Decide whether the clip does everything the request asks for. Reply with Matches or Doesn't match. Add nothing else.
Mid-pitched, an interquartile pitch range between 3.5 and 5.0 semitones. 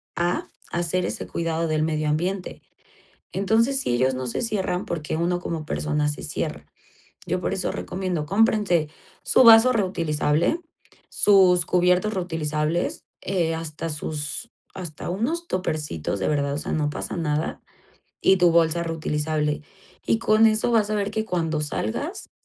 Matches